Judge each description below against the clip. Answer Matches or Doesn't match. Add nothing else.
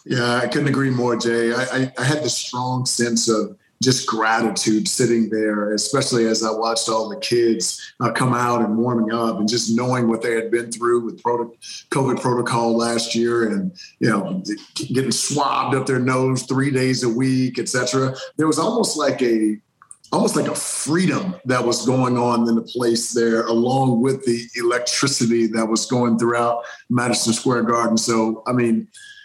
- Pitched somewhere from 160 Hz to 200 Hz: Doesn't match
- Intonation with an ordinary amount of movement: Doesn't match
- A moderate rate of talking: Matches